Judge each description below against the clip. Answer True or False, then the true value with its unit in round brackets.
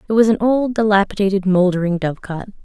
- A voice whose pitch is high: True (200 Hz)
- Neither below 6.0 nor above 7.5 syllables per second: True (6.5 syllables/s)